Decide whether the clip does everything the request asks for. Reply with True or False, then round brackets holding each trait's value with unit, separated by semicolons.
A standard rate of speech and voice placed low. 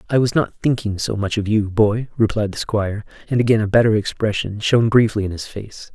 False (220 wpm; 110 Hz)